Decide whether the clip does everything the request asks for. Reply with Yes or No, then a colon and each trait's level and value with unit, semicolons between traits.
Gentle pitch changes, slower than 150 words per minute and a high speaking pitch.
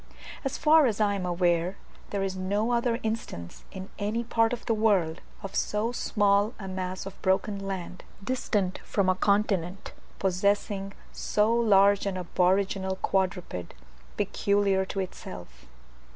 Yes: narrow, 2.2 semitones; average, 140 wpm; high, 195 Hz